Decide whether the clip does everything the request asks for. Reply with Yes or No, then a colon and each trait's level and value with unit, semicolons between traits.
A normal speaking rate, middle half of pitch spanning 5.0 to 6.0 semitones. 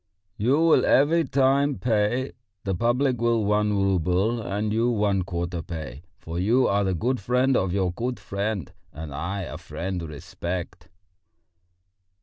Yes: average, 145 wpm; average, 5.3 semitones